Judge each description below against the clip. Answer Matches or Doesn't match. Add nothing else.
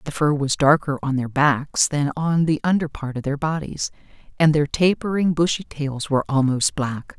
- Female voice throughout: Matches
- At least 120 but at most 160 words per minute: Doesn't match